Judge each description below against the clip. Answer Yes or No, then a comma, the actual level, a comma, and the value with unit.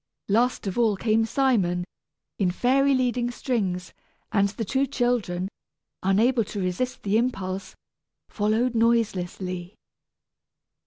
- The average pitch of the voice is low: No, high, 220 Hz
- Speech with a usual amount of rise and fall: Yes, average, 4.5 semitones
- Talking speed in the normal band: No, slow, 110 wpm